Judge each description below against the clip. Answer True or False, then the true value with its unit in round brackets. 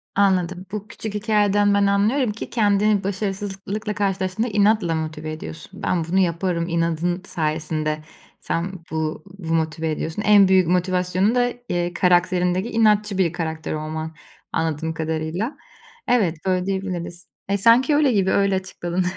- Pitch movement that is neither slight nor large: True (3.6 semitones)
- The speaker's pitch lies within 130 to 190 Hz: True (185 Hz)